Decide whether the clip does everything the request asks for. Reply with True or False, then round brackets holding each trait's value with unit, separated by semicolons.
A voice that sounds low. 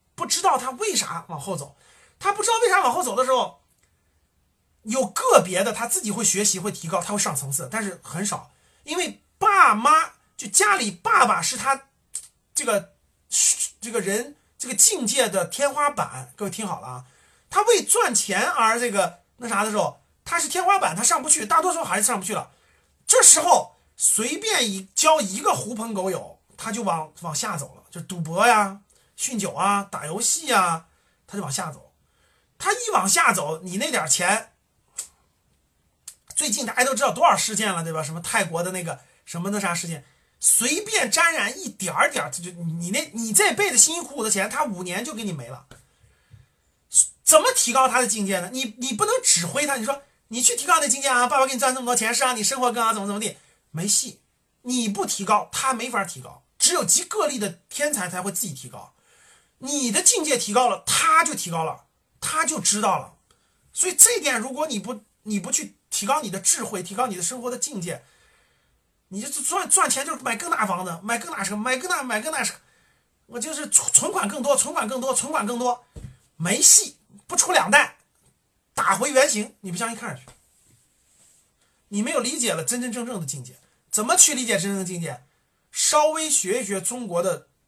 False (235 Hz)